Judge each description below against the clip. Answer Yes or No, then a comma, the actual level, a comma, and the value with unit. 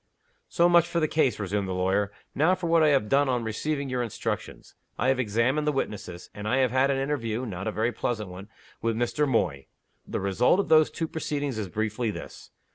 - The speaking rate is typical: No, fast, 215 wpm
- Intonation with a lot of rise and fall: Yes, wide, 5.8 semitones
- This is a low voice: Yes, low, 125 Hz